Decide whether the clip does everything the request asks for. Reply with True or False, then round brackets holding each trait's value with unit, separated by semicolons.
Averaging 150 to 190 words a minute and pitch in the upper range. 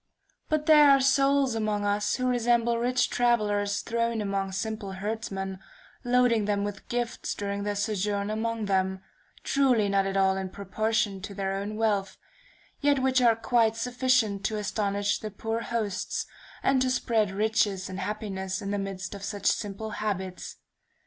True (160 wpm; 210 Hz)